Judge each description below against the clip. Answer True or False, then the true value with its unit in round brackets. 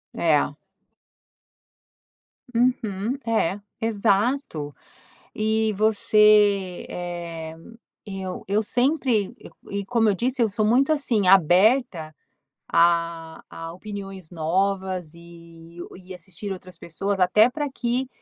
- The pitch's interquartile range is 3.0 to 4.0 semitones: False (4.4 semitones)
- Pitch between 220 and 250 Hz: False (195 Hz)